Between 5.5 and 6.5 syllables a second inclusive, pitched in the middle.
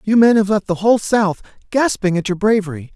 No: 5.8 syllables/s; high, 200 Hz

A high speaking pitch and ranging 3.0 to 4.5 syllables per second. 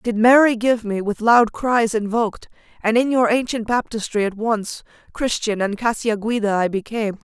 No: high, 220 Hz; 5.0 syllables/s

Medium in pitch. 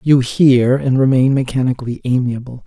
No: low, 130 Hz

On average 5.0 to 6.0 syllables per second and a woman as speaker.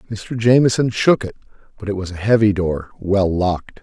No: 5.2 syllables/s; male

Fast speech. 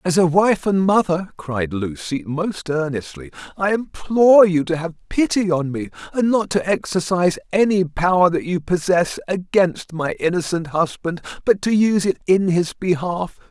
No: average, 165 wpm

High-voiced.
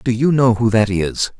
No: low, 115 Hz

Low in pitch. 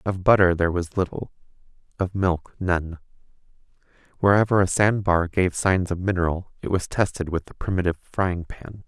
Yes: very low, 90 Hz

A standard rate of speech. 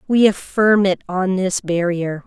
Yes: average, 160 wpm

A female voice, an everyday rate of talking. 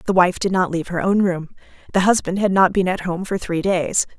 No: female; fast, 260 wpm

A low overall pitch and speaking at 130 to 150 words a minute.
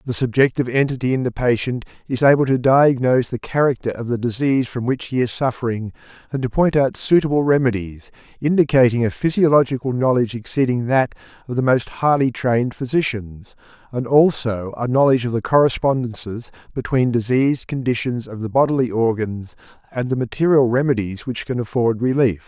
No: low, 125 Hz; average, 160 wpm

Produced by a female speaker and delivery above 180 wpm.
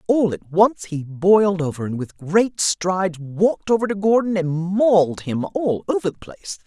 Yes: female; average, 190 wpm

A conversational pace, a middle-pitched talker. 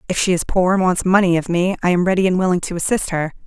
No: fast, 295 wpm; medium, 180 Hz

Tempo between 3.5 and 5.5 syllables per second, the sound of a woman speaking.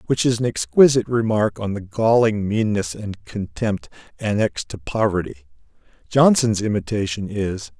No: 4.9 syllables/s; male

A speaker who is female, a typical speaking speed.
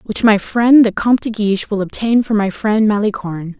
No: female; fast, 215 wpm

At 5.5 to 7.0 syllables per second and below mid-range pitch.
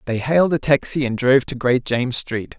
Yes: 5.8 syllables/s; low, 130 Hz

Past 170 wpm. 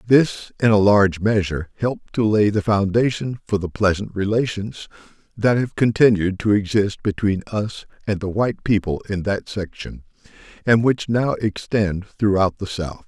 No: average, 160 wpm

